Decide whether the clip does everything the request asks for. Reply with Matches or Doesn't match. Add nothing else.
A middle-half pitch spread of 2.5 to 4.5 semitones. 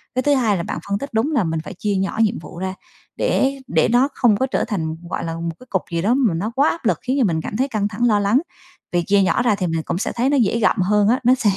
Doesn't match